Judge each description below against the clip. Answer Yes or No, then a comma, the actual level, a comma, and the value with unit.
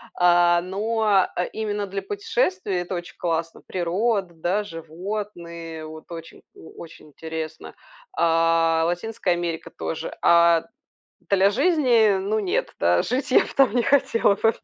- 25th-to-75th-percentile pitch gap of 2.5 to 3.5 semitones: No, average, 4.4 semitones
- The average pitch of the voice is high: No, medium, 180 Hz